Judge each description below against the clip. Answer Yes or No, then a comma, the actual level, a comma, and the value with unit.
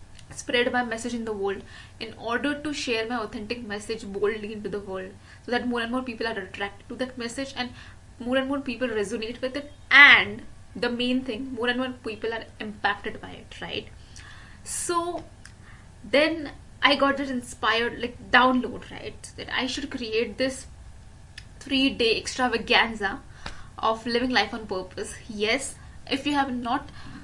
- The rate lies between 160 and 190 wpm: Yes, average, 165 wpm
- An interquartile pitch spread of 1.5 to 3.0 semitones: Yes, average, 2.7 semitones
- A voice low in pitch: No, high, 245 Hz